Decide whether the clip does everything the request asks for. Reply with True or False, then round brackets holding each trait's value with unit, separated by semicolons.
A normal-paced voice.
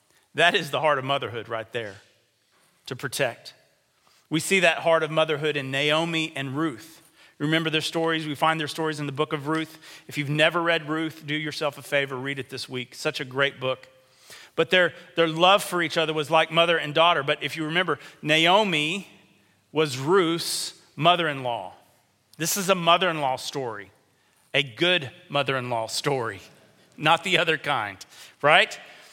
True (185 wpm)